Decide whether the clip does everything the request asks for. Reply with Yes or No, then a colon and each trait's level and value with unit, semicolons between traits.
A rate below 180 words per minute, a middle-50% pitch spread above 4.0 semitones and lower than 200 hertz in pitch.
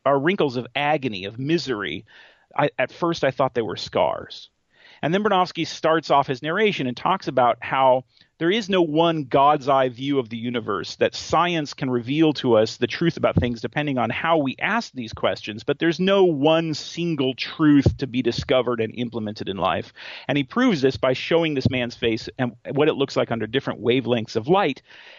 No: average, 200 wpm; average, 4.7 semitones; low, 135 Hz